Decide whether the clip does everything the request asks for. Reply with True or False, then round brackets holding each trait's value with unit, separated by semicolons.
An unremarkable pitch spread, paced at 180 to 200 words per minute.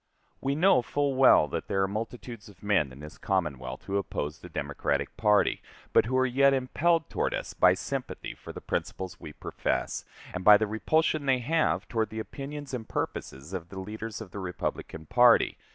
False (6.0 semitones; 190 wpm)